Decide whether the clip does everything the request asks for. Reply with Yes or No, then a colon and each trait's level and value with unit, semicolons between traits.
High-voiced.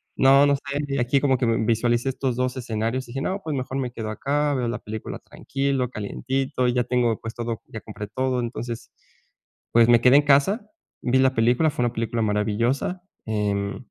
No: low, 125 Hz